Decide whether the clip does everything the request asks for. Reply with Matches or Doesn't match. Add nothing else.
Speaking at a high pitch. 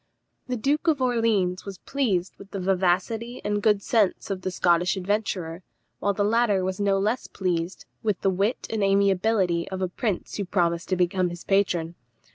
Matches